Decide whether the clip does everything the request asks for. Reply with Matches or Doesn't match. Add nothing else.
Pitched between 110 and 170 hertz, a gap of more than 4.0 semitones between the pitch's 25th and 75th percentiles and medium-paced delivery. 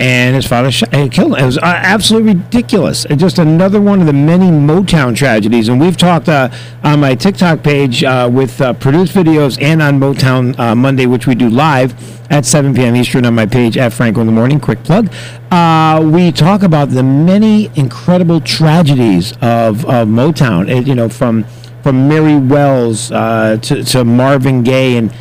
Matches